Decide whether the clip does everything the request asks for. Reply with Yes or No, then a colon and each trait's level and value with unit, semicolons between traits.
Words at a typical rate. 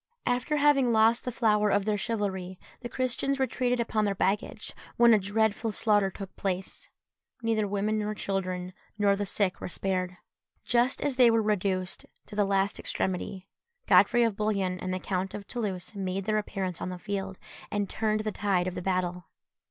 Yes: average, 175 wpm